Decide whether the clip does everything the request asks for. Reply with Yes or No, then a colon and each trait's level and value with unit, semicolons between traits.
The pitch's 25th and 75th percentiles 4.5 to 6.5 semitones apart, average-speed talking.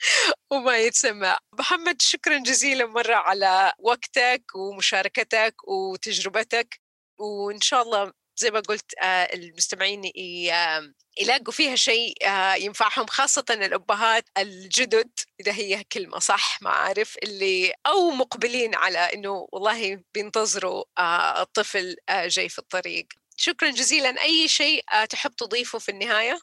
Yes: average, 5.2 semitones; average, 110 wpm